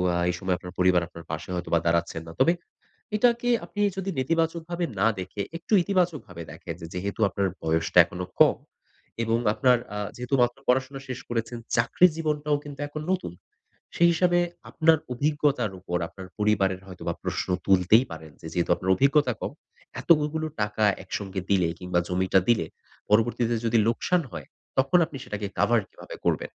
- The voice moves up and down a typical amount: No, wide, 8.5 semitones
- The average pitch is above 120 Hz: No, low, 115 Hz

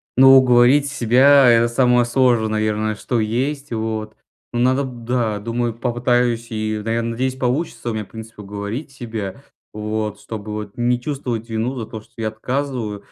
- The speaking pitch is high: No, low, 115 Hz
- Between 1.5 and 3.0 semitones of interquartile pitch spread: Yes, narrow, 2.6 semitones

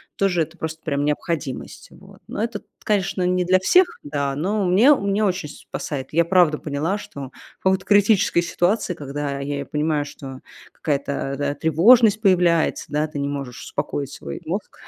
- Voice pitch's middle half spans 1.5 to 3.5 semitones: No, average, 4.9 semitones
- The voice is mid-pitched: Yes, medium, 160 Hz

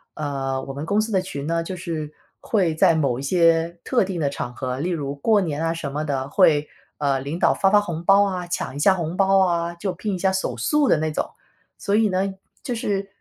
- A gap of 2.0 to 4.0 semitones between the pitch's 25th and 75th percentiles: No, average, 4.8 semitones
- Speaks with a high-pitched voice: No, medium, 170 Hz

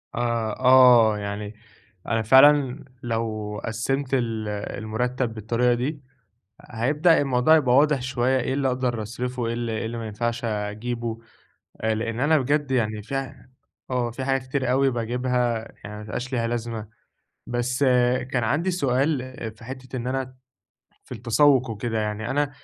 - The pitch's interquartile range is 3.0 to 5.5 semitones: No, narrow, 2.6 semitones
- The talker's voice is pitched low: Yes, low, 125 Hz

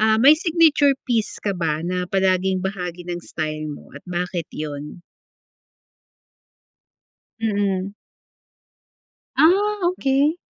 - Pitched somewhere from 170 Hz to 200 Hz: Yes, high, 190 Hz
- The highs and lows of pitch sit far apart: Yes, wide, 7.9 semitones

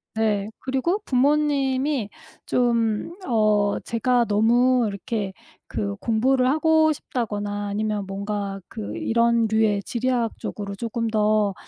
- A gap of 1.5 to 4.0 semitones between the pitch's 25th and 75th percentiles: Yes, average, 3.6 semitones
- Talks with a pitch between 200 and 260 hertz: Yes, high, 225 Hz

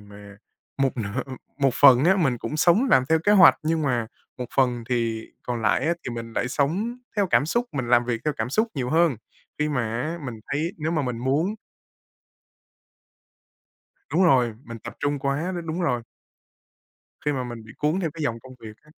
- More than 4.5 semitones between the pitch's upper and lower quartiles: Yes, average, 5.1 semitones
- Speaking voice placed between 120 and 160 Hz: Yes, low, 135 Hz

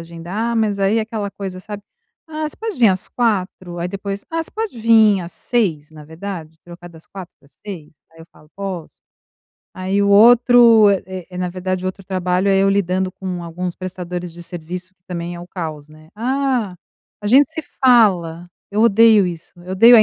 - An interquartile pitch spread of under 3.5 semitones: No, average, 3.8 semitones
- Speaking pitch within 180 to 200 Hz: Yes, high, 190 Hz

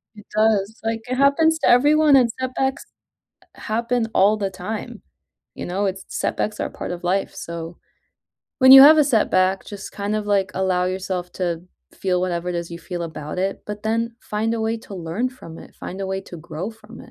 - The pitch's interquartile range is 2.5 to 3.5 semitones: No, average, 4.1 semitones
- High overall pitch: Yes, high, 205 Hz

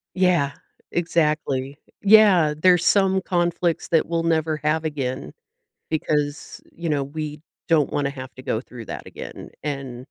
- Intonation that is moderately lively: Yes, average, 3.4 semitones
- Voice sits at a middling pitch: Yes, medium, 155 Hz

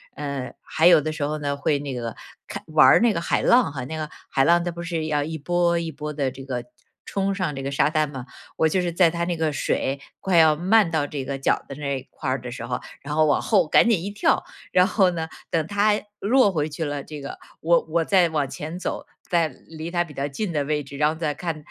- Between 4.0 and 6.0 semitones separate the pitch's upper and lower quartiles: No, average, 3.2 semitones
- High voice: No, medium, 155 Hz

